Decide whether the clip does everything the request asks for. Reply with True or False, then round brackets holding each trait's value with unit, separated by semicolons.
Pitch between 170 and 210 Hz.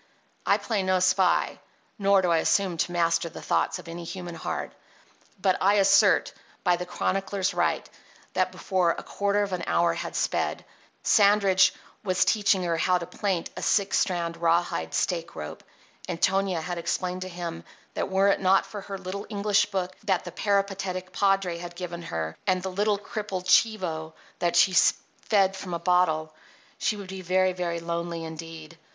True (185 Hz)